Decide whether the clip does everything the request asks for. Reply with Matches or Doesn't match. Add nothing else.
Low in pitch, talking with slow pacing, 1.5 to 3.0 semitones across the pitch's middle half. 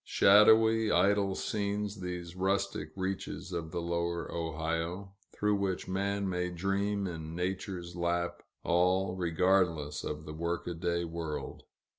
Matches